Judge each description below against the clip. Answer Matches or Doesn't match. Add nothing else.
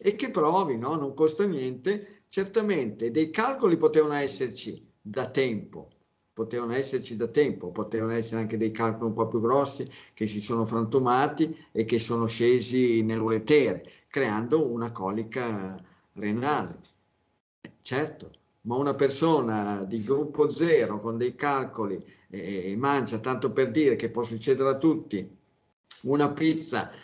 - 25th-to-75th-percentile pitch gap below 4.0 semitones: Doesn't match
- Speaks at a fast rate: Doesn't match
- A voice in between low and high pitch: Doesn't match